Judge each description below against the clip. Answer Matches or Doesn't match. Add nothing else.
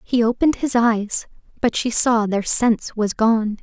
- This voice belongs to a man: Doesn't match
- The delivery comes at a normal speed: Matches